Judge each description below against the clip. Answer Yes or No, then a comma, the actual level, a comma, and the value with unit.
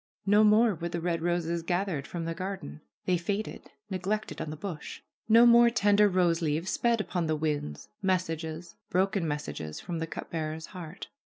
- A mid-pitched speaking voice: Yes, medium, 175 Hz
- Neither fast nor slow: Yes, average, 180 wpm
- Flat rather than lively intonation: No, average, 3.6 semitones